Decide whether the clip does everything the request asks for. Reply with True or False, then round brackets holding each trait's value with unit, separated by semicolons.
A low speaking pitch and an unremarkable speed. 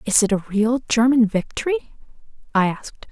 False (230 Hz; 155 wpm)